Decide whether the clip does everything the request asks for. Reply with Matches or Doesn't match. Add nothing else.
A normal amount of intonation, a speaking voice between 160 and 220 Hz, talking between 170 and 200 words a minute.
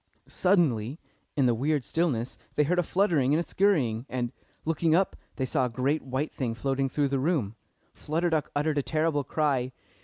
Doesn't match